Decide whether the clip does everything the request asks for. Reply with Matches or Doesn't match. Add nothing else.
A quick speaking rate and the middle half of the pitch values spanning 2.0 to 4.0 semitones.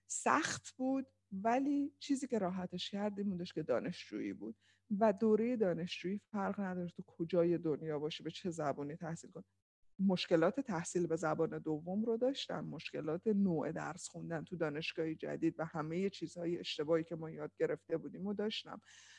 Doesn't match